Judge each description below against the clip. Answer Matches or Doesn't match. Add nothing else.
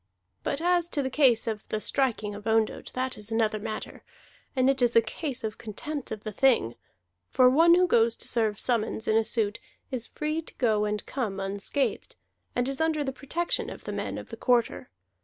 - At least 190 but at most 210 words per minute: Matches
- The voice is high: Matches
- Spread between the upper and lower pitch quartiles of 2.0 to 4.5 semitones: Matches